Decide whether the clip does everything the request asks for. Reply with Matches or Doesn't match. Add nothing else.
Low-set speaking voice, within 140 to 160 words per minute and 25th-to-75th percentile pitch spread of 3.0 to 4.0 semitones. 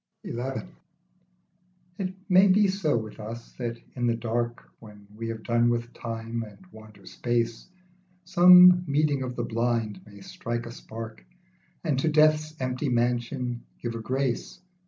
Matches